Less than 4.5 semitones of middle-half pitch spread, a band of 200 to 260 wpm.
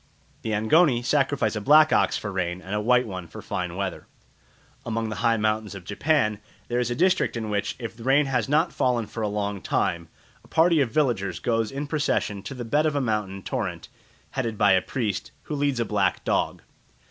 No: average, 5.0 semitones; fast, 205 wpm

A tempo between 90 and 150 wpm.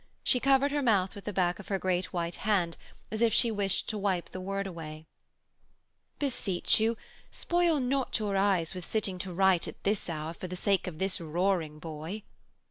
No: average, 195 wpm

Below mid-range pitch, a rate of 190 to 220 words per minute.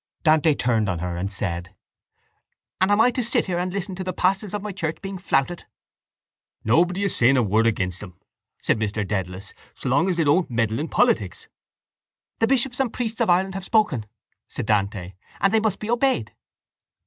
No: medium, 165 Hz; average, 195 wpm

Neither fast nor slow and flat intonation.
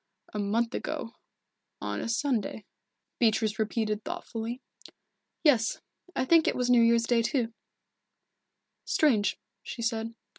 No: slow, 120 wpm; narrow, 1.9 semitones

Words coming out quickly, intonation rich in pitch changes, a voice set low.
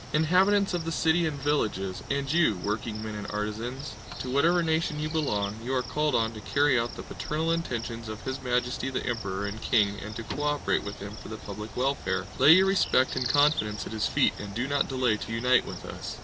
Yes: fast, 220 wpm; wide, 5.7 semitones; low, 125 Hz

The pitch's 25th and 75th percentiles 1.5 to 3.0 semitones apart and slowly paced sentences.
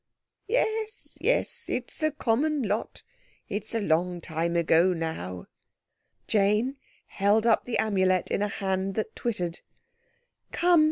No: average, 5.0 semitones; slow, 130 wpm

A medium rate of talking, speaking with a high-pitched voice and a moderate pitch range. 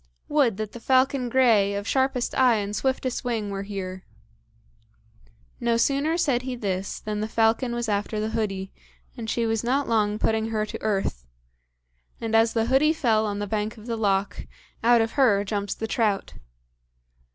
Yes: average, 175 wpm; high, 225 Hz; average, 3.0 semitones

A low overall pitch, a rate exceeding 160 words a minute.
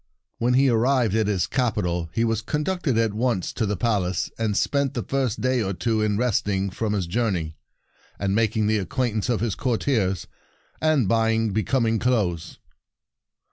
Yes: low, 110 Hz; average, 170 wpm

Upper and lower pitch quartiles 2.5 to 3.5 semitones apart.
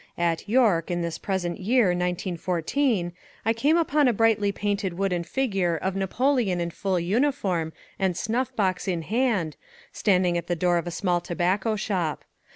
No: average, 4.2 semitones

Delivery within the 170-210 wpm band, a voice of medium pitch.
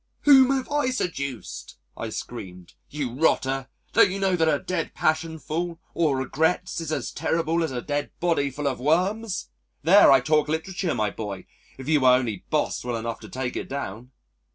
Yes: average, 180 wpm; medium, 150 Hz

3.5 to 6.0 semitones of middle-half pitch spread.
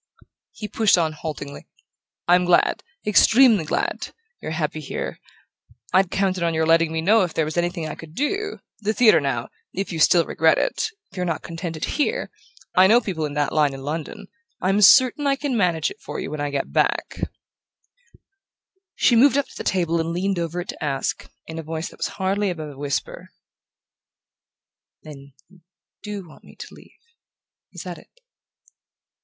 Yes: average, 4.8 semitones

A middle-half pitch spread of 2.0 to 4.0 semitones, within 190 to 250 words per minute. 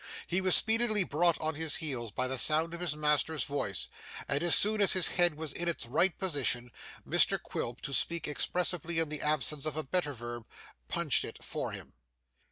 Yes: average, 3.7 semitones; average, 195 wpm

